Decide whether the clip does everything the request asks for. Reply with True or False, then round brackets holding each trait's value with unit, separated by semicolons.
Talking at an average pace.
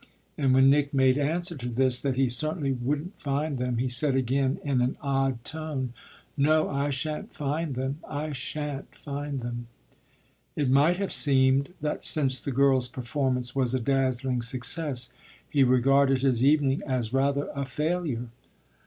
True (160 wpm)